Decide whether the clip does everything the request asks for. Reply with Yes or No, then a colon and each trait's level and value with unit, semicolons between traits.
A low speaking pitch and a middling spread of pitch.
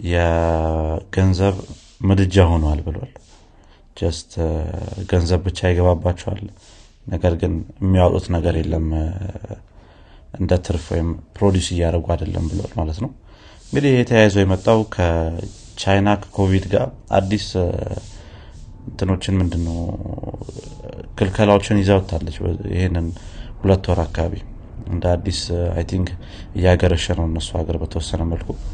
Yes: very low, 90 Hz; average, 3.2 semitones